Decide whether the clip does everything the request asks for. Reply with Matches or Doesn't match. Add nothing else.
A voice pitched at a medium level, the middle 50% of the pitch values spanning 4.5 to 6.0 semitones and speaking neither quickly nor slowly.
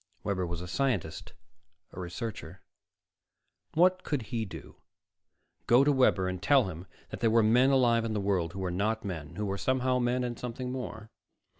Doesn't match